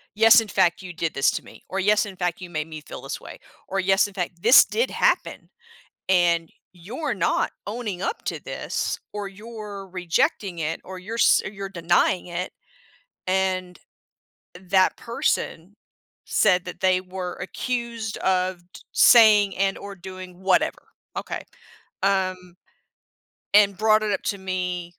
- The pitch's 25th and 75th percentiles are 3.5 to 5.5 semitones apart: No, narrow, 2.5 semitones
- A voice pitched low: No, high, 190 Hz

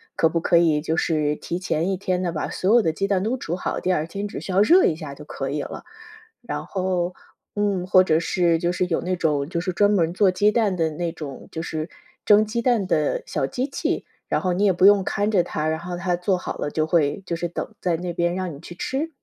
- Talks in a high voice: No, medium, 180 Hz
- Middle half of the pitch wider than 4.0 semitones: No, average, 3.1 semitones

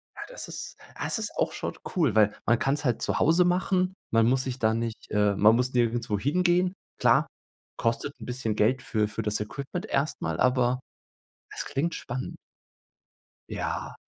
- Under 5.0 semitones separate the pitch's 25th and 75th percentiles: No, wide, 5.6 semitones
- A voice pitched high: No, low, 125 Hz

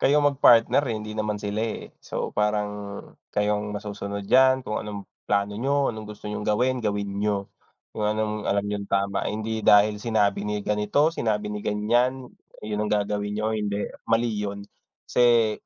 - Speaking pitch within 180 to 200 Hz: No, low, 105 Hz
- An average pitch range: No, narrow, 1.4 semitones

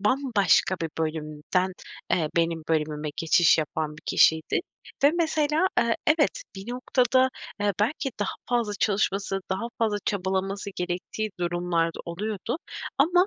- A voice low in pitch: No, high, 195 Hz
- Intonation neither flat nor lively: No, wide, 6.4 semitones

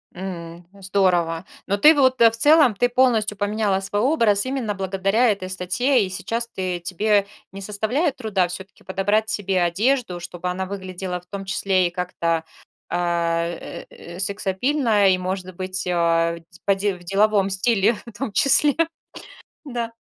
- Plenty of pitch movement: No, average, 3.4 semitones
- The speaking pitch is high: Yes, high, 195 Hz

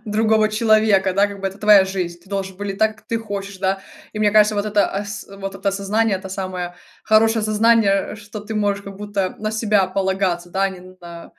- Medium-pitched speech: No, high, 200 Hz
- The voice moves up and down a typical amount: No, narrow, 1.8 semitones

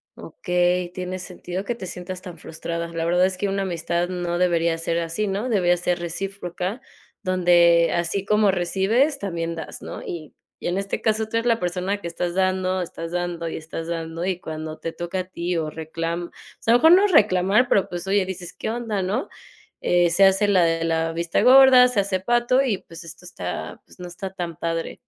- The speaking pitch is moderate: Yes, medium, 180 Hz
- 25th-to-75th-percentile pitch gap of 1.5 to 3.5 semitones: Yes, average, 2.7 semitones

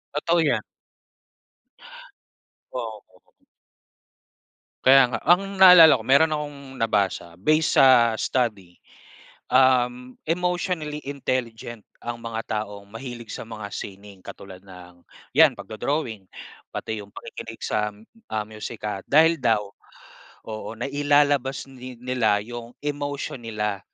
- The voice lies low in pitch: Yes, low, 120 Hz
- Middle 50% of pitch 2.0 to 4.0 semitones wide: No, average, 5.0 semitones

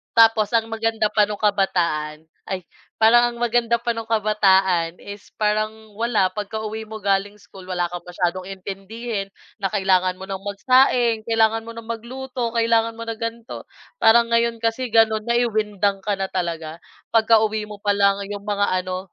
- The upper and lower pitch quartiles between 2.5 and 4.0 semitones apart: Yes, average, 2.8 semitones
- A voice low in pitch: No, high, 215 Hz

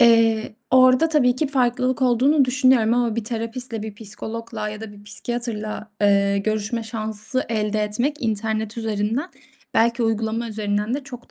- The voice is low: No, high, 225 Hz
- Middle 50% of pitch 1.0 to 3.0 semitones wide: Yes, narrow, 2.5 semitones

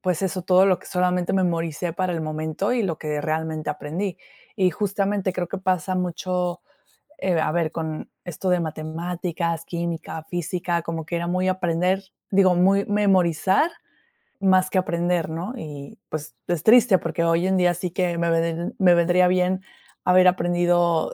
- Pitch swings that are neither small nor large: No, narrow, 2.0 semitones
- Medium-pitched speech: Yes, medium, 175 Hz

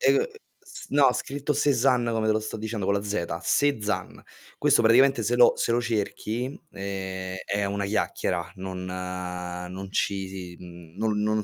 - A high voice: No, low, 100 Hz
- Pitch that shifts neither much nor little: Yes, average, 4.0 semitones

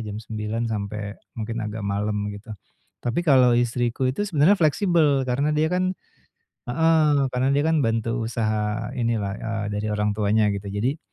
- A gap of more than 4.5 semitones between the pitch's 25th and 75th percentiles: Yes, average, 5.0 semitones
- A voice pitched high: No, low, 115 Hz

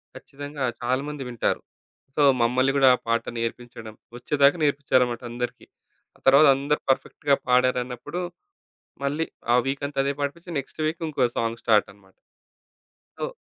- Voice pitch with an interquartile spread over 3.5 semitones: No, average, 2.8 semitones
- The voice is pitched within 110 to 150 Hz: Yes, low, 135 Hz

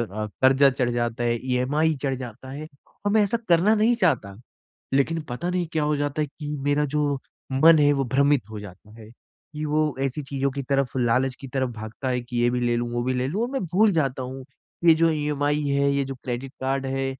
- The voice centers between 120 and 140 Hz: Yes, low, 135 Hz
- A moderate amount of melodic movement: Yes, average, 3.2 semitones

